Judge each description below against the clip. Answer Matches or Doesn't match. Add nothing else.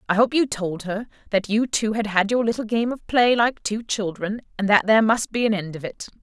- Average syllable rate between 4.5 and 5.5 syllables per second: Matches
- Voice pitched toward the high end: Matches